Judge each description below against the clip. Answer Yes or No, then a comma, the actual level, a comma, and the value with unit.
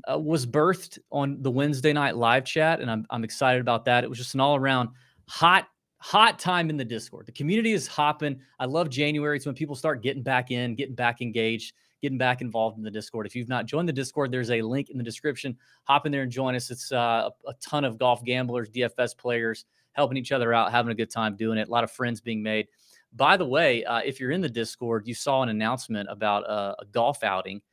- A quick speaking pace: Yes, fast, 240 wpm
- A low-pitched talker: Yes, low, 125 Hz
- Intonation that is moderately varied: Yes, average, 3.7 semitones